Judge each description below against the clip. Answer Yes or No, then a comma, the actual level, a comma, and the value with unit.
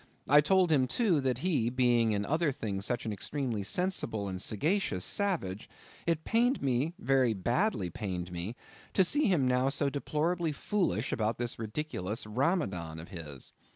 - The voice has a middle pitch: No, low, 125 Hz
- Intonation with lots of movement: Yes, wide, 8.0 semitones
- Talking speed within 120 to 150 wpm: No, average, 160 wpm